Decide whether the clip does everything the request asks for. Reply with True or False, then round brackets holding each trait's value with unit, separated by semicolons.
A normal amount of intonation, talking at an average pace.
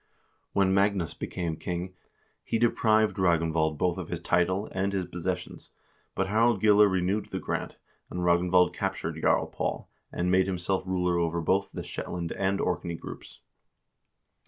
False (2.1 semitones; 155 wpm)